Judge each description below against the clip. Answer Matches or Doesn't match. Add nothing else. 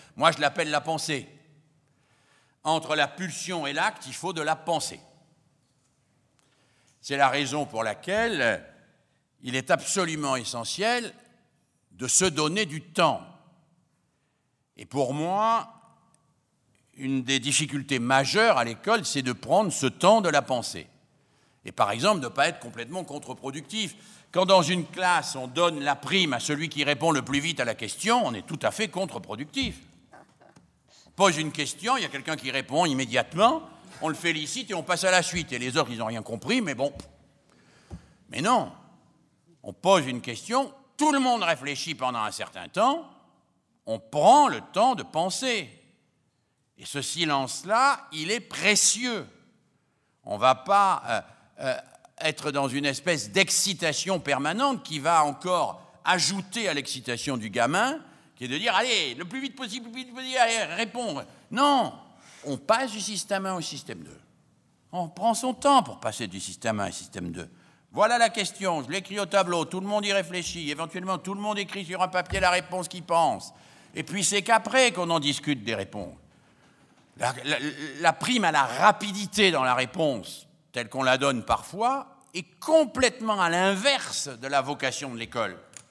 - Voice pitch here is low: Doesn't match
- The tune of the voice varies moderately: Doesn't match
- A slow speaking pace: Doesn't match